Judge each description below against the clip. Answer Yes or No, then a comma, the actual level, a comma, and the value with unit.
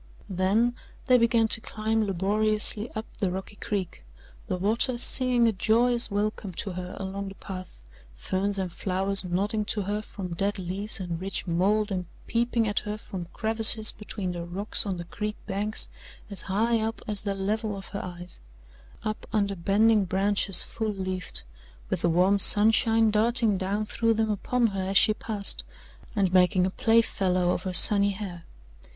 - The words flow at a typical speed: Yes, average, 170 wpm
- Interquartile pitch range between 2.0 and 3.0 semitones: Yes, narrow, 2.6 semitones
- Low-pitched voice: No, high, 200 Hz